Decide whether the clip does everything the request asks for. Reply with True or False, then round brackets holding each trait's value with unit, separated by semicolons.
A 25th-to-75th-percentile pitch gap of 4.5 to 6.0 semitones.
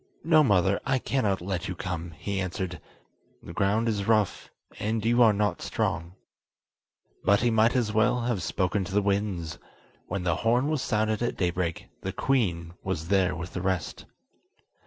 False (3.9 semitones)